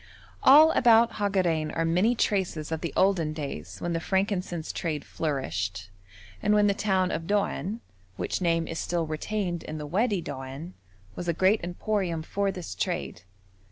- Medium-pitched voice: Yes, medium, 175 Hz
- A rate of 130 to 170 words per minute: Yes, average, 160 wpm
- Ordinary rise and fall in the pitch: Yes, average, 4.2 semitones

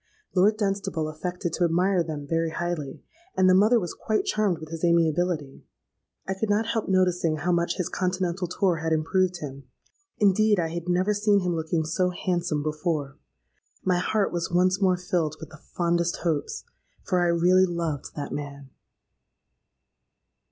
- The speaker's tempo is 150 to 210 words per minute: Yes, average, 160 wpm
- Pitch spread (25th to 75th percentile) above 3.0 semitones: No, narrow, 2.6 semitones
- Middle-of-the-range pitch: Yes, medium, 175 Hz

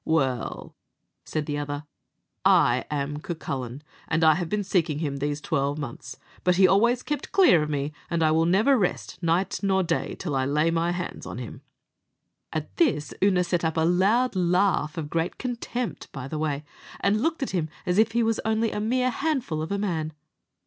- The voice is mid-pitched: Yes, medium, 170 Hz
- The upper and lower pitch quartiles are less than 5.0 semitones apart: No, average, 5.3 semitones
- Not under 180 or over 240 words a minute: Yes, average, 195 wpm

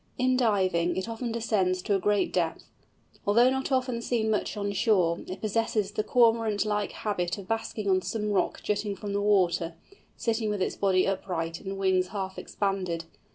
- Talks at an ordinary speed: Yes, average, 180 wpm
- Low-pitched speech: No, high, 205 Hz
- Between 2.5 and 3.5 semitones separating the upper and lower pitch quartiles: Yes, average, 3.1 semitones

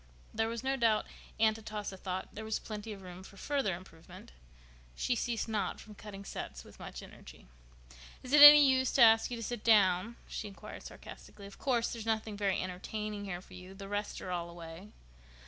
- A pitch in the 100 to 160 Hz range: No, high, 210 Hz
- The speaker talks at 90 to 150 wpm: No, average, 200 wpm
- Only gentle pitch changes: No, average, 3.2 semitones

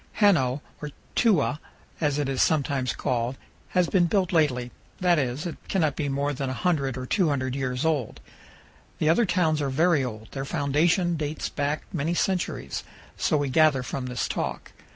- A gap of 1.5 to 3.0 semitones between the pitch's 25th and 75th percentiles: No, average, 4.1 semitones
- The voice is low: No, medium, 145 Hz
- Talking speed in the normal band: Yes, average, 170 wpm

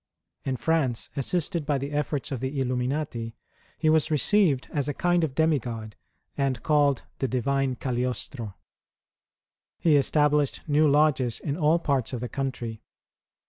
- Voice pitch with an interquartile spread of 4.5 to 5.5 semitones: No, average, 3.0 semitones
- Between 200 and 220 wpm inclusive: No, average, 140 wpm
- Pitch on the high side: No, medium, 140 Hz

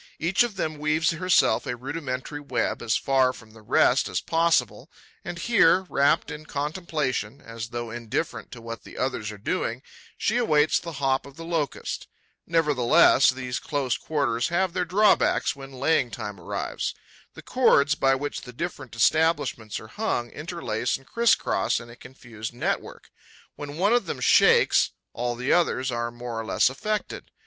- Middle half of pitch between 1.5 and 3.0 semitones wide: No, wide, 5.5 semitones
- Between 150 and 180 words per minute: Yes, average, 170 wpm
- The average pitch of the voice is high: No, medium, 140 Hz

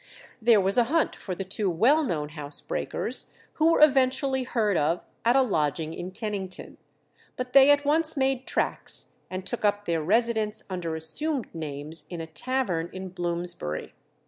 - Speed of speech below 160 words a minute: No, average, 170 wpm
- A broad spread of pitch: Yes, wide, 7.6 semitones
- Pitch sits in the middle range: No, high, 205 Hz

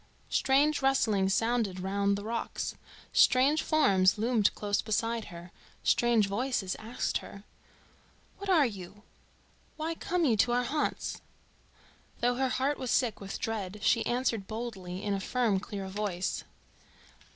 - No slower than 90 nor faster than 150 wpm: Yes, average, 140 wpm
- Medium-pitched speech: No, high, 225 Hz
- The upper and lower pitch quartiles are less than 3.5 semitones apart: No, average, 4.2 semitones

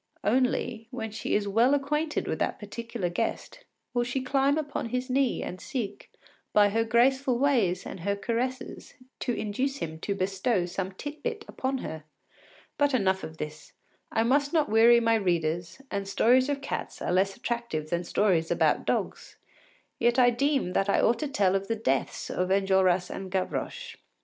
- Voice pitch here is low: No, high, 225 Hz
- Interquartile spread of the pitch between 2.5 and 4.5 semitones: No, wide, 5.4 semitones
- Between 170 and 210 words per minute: Yes, average, 175 wpm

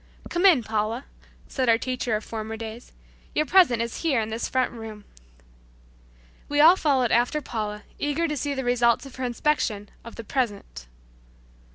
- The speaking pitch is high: Yes, high, 240 Hz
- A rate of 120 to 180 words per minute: Yes, average, 175 wpm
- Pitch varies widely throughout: No, average, 4.2 semitones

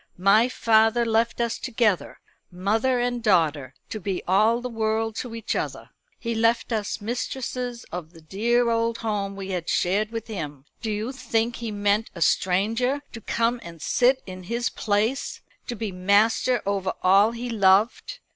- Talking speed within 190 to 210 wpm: No, average, 165 wpm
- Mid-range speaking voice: No, high, 220 Hz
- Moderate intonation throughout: Yes, average, 3.2 semitones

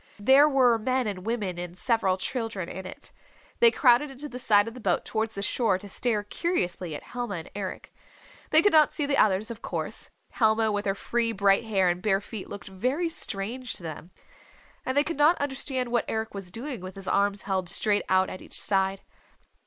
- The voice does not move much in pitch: No, average, 4.7 semitones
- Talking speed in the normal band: No, fast, 210 wpm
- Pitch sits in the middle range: No, high, 215 Hz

